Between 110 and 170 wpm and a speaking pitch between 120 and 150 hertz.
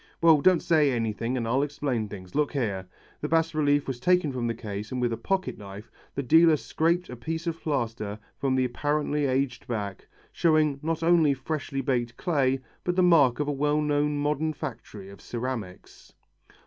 No: average, 185 wpm; medium, 140 Hz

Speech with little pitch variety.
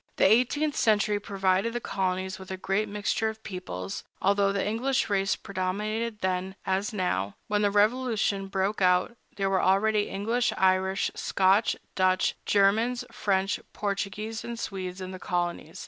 Yes: narrow, 2.3 semitones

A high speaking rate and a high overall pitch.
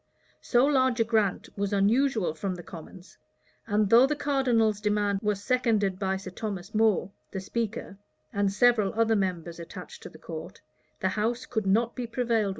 No: average, 190 wpm; high, 210 Hz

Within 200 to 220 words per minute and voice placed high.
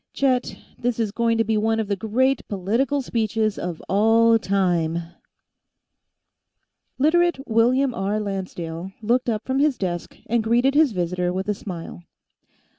No: average, 150 wpm; high, 220 Hz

